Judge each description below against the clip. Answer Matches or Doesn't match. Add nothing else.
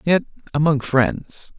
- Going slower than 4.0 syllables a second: Matches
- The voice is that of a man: Matches